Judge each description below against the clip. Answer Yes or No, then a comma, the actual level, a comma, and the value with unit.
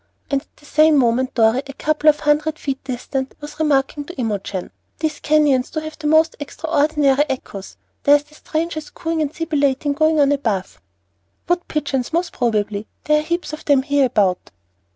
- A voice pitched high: Yes, very high, 290 Hz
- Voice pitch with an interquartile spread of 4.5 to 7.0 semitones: No, average, 2.9 semitones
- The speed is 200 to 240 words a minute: No, average, 175 wpm